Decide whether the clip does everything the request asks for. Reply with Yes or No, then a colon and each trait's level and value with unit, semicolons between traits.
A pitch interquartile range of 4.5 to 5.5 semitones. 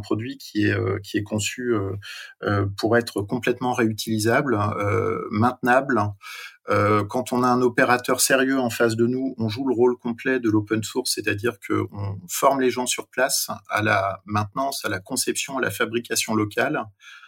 No: average, 3.2 semitones